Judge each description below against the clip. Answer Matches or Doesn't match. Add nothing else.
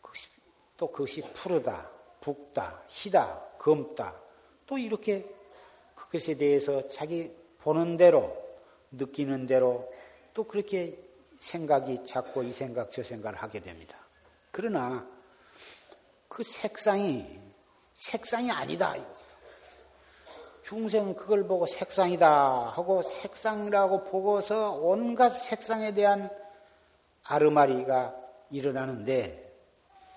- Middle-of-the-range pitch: Matches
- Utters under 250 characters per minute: Matches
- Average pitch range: Doesn't match